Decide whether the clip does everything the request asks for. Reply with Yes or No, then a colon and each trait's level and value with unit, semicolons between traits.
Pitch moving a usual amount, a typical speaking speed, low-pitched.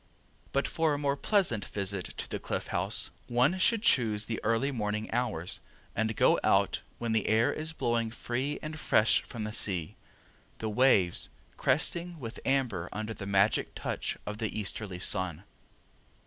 Yes: average, 4.7 semitones; average, 160 wpm; low, 110 Hz